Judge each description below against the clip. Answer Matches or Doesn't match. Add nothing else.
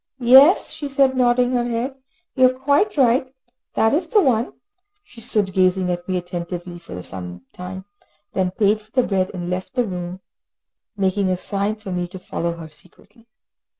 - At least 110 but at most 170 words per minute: Doesn't match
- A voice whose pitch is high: Matches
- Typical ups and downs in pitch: Doesn't match